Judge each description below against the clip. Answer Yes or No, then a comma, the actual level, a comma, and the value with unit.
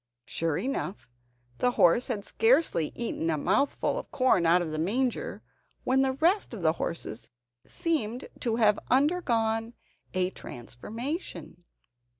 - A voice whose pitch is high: Yes, high, 225 Hz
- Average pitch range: No, wide, 7.6 semitones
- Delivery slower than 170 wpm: Yes, slow, 135 wpm